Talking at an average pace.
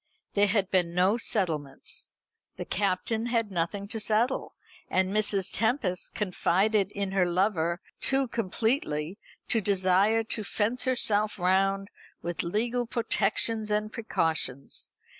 No: slow, 120 wpm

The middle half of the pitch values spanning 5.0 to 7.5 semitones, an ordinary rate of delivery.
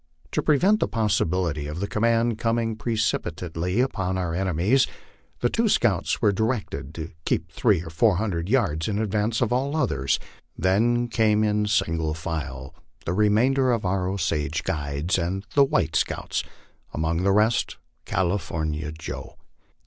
Yes: wide, 5.6 semitones; average, 150 wpm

